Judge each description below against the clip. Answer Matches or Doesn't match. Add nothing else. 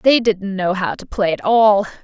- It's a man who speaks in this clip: Doesn't match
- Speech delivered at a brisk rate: Matches